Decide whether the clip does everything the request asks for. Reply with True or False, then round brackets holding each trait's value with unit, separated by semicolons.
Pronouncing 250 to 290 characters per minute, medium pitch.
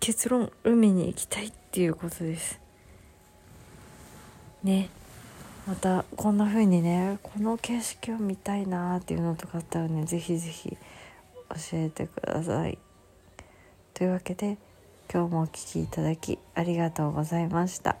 True (285 characters per minute; 170 Hz)